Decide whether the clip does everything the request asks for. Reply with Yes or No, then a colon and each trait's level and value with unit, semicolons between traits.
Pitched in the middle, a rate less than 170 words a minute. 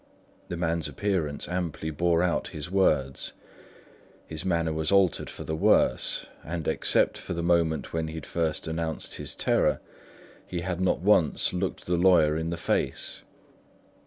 No: very low, 85 Hz; average, 160 wpm